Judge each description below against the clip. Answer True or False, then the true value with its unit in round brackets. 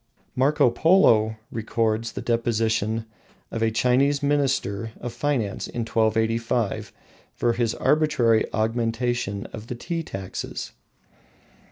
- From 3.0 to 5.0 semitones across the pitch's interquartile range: False (2.4 semitones)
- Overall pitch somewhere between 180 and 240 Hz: False (115 Hz)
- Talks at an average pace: False (110 wpm)